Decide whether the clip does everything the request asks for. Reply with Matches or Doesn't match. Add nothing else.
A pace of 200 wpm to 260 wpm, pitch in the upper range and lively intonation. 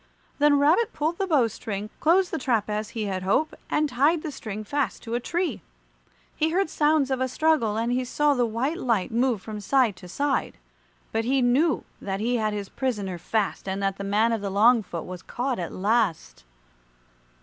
Matches